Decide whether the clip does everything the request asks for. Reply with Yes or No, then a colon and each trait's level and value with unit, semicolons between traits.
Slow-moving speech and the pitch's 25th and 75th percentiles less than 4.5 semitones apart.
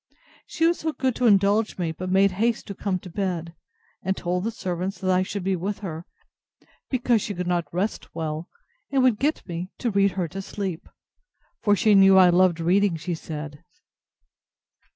No: average, 195 wpm; average, 2.8 semitones